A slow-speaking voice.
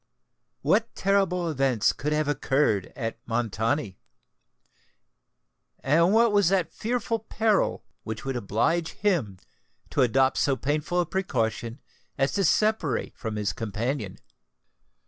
Yes: slow, 120 wpm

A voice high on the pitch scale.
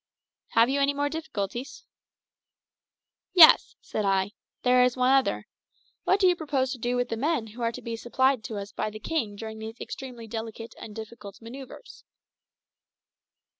Yes: high, 240 Hz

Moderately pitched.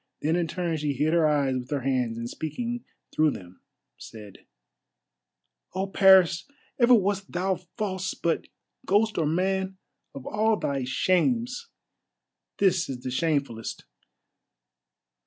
Yes: medium, 170 Hz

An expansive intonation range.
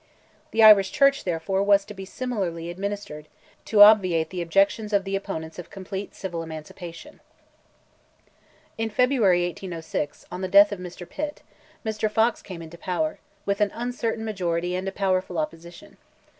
No: average, 3.5 semitones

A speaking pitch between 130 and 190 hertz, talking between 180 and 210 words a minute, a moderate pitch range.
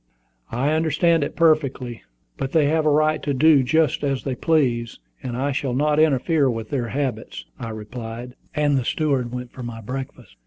Yes: low, 135 Hz; average, 185 wpm; average, 3.8 semitones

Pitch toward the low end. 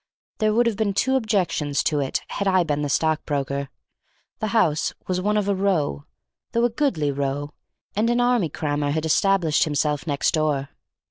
No: medium, 160 Hz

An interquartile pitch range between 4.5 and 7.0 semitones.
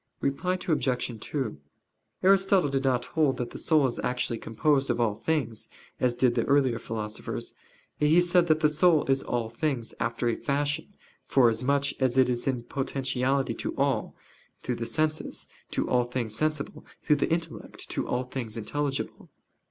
No: average, 3.9 semitones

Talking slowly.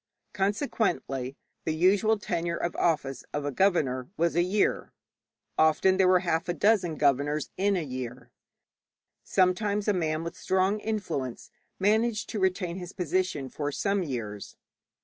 No: average, 145 wpm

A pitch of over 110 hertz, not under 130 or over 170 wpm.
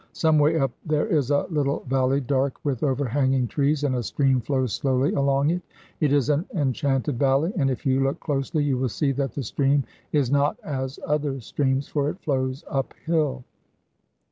No: medium, 140 Hz; average, 185 wpm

